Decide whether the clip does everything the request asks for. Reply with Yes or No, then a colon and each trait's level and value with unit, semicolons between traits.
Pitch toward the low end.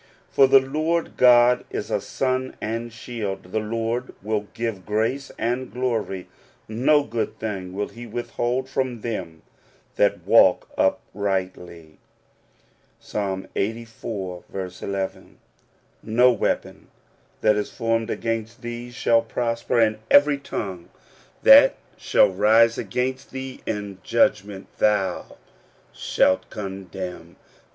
Yes: low, 115 Hz